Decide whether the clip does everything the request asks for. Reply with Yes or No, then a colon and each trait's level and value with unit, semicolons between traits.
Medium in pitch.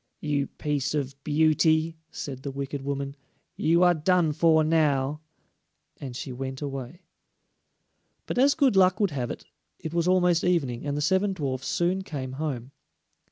Yes: medium, 150 Hz